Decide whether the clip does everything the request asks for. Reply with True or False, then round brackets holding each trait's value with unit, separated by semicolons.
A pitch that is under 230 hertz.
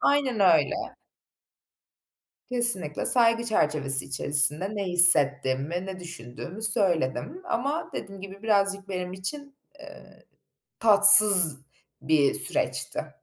True (190 Hz)